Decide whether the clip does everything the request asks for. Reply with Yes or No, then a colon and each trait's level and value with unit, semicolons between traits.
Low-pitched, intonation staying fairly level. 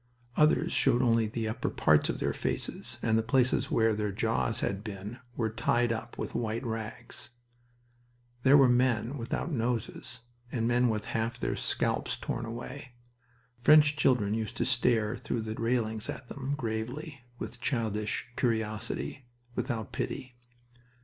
Yes: low, 115 Hz; narrow, 2.2 semitones